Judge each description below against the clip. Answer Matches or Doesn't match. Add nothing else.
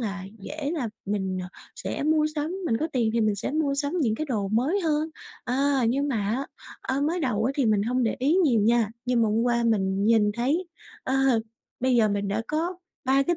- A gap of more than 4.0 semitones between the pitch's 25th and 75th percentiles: Matches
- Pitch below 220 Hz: Doesn't match